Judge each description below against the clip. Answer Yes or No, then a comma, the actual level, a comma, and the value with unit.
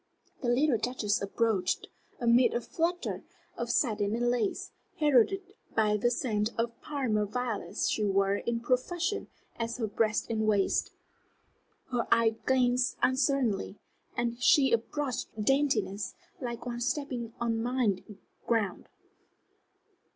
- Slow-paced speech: Yes, slow, 130 wpm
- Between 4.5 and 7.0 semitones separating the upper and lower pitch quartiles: No, average, 3.1 semitones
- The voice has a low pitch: No, high, 235 Hz